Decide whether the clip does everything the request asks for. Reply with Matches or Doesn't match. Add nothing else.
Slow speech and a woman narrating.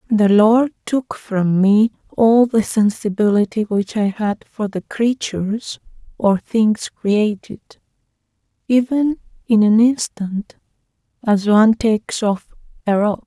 Matches